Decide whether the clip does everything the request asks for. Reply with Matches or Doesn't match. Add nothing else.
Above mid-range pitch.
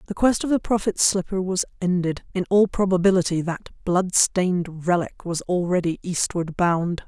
Doesn't match